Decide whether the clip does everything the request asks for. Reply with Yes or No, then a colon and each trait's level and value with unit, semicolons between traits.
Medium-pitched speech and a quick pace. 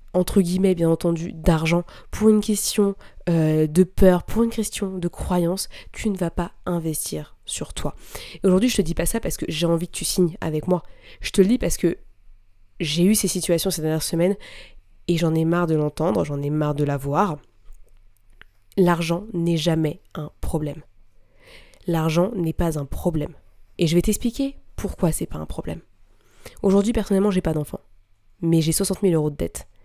No: medium, 170 Hz; average, 190 wpm